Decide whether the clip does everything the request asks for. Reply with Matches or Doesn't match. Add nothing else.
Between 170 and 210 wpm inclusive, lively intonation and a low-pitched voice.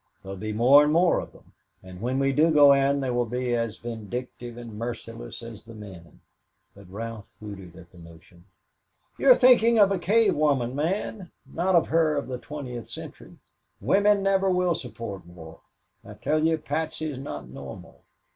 Matches